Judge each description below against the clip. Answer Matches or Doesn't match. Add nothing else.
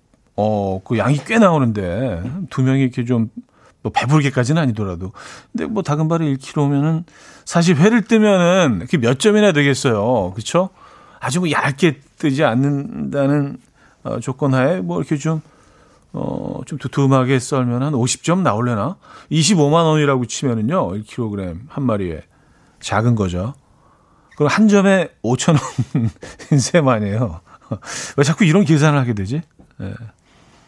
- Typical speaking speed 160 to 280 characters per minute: Matches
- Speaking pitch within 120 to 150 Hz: Matches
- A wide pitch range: Doesn't match